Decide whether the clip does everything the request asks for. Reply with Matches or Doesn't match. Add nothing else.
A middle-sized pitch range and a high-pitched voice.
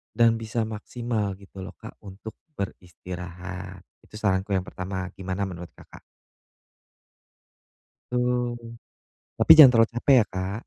Doesn't match